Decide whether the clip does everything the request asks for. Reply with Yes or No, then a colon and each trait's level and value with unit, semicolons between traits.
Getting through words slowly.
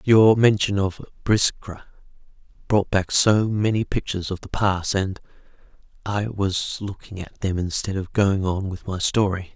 No: average, 150 wpm